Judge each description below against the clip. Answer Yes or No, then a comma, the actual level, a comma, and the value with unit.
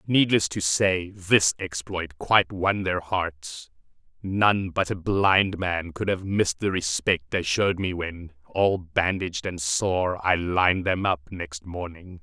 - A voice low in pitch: Yes, very low, 90 Hz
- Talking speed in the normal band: Yes, average, 160 wpm